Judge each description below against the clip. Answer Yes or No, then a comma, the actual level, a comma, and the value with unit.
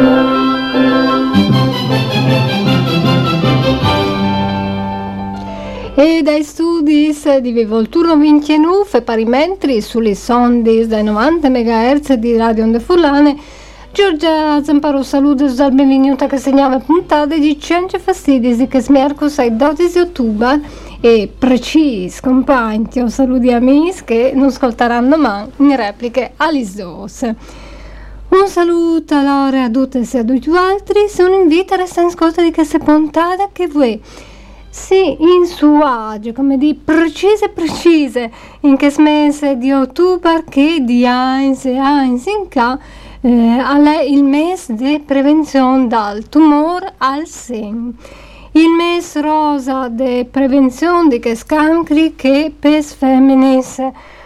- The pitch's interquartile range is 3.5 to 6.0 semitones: Yes, average, 4.1 semitones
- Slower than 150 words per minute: Yes, average, 120 wpm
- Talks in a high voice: Yes, very high, 275 Hz